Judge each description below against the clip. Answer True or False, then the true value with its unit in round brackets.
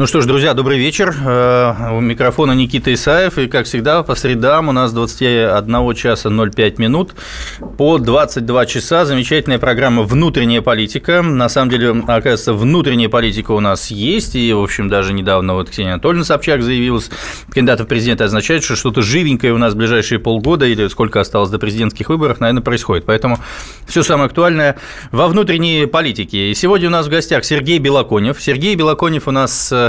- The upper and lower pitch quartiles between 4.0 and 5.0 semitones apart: True (4.3 semitones)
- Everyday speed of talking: False (175 wpm)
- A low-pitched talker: True (125 Hz)